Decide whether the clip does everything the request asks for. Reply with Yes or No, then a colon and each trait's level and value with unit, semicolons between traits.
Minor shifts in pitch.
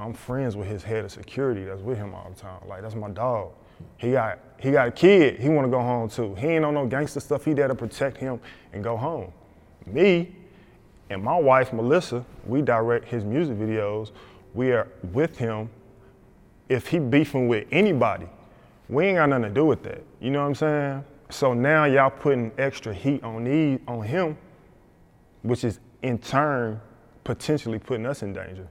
No: average, 4.5 semitones